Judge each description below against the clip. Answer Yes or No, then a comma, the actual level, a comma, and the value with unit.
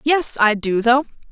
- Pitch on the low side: No, high, 245 Hz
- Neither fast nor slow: Yes, average, 185 wpm